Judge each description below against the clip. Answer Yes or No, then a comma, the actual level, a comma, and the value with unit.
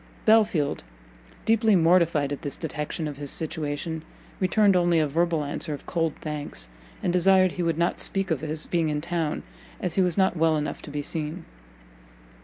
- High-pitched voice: No, medium, 165 Hz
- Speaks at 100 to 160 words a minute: No, average, 180 wpm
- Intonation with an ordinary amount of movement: Yes, average, 3.0 semitones